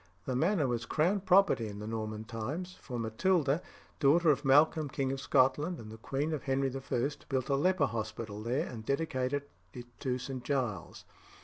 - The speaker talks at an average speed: Yes, average, 180 wpm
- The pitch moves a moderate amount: Yes, average, 4.6 semitones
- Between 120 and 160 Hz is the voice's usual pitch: Yes, low, 135 Hz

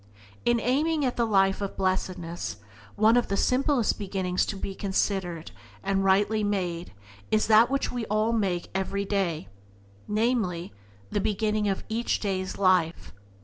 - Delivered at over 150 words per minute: No, average, 145 wpm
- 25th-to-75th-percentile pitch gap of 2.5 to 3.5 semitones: Yes, average, 2.9 semitones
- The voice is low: No, high, 200 Hz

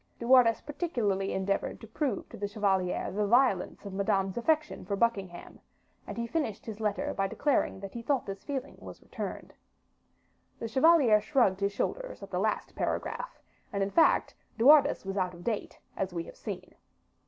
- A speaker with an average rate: Yes, average, 180 wpm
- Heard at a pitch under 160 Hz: No, high, 215 Hz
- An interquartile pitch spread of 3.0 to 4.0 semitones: No, average, 5.1 semitones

